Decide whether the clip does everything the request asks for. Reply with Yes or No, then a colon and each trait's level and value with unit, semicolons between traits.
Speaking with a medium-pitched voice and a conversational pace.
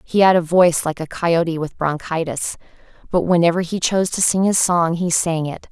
No: medium, 170 Hz; fast, 210 wpm